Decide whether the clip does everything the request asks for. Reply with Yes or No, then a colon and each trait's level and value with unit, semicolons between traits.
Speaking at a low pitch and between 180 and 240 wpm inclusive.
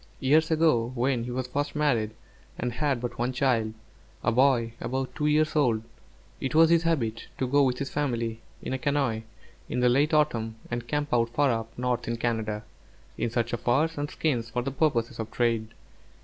Yes: low, 125 Hz; average, 190 wpm